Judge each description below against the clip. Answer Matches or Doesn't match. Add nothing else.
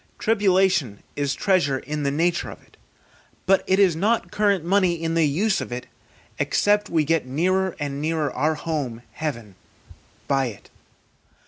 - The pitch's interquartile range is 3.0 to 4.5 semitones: Doesn't match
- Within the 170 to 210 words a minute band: Doesn't match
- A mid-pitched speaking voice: Matches